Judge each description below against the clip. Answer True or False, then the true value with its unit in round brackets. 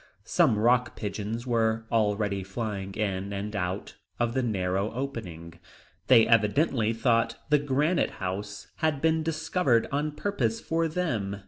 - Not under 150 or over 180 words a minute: False (135 wpm)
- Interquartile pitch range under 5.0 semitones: False (5.3 semitones)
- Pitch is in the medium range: False (115 Hz)